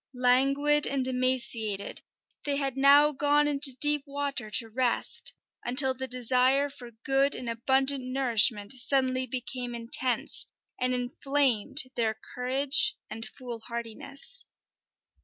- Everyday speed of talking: No, slow, 115 wpm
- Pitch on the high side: Yes, very high, 260 Hz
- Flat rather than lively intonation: Yes, narrow, 2.3 semitones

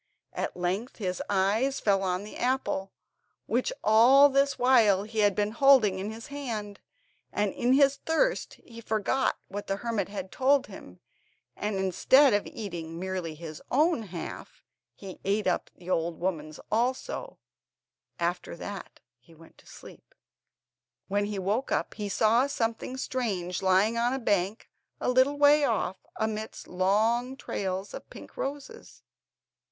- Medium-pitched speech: No, high, 210 Hz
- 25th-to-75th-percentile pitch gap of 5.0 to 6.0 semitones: Yes, average, 5.3 semitones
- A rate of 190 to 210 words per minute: No, average, 150 wpm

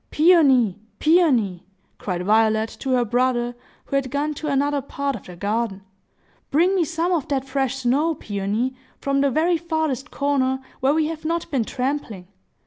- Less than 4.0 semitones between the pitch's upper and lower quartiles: No, average, 4.6 semitones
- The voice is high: Yes, very high, 270 Hz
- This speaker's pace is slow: No, average, 165 wpm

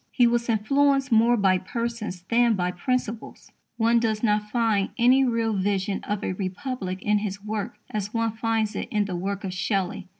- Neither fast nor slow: Yes, average, 185 wpm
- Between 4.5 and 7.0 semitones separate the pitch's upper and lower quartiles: No, average, 3.0 semitones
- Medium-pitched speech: No, high, 215 Hz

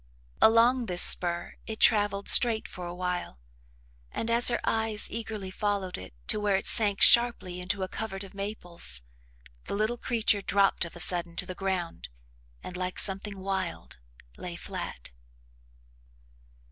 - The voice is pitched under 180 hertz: No, high, 195 Hz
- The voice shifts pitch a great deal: No, average, 3.3 semitones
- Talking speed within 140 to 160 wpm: Yes, average, 150 wpm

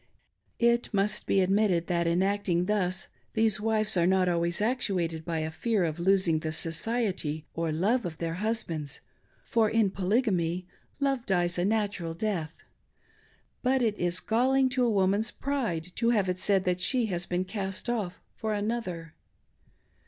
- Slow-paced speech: No, average, 165 wpm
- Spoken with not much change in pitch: No, average, 4.3 semitones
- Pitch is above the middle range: Yes, high, 195 Hz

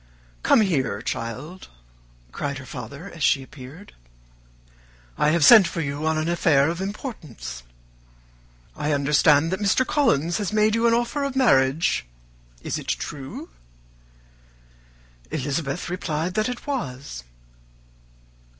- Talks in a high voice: No, medium, 160 Hz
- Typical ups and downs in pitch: No, wide, 6.7 semitones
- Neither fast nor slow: No, slow, 125 wpm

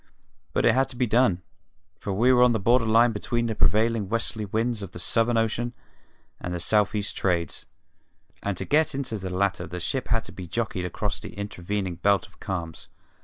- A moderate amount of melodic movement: Yes, average, 3.9 semitones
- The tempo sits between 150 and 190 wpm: No, fast, 205 wpm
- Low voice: Yes, low, 105 Hz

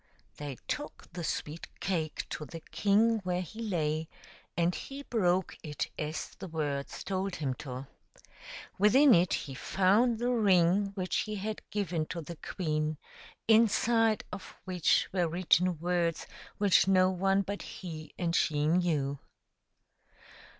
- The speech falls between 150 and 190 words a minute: No, average, 140 wpm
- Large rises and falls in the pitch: No, average, 4.2 semitones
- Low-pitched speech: No, medium, 180 Hz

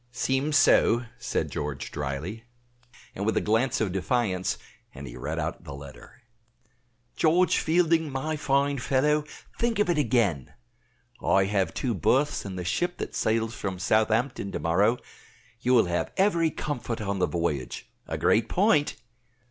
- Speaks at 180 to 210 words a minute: No, average, 155 wpm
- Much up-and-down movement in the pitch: Yes, wide, 7.7 semitones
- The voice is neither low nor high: No, low, 115 Hz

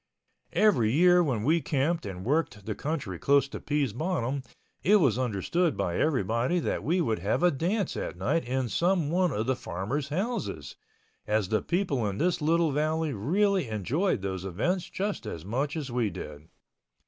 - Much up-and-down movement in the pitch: Yes, wide, 7.9 semitones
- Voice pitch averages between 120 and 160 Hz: Yes, medium, 140 Hz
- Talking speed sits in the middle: Yes, average, 175 wpm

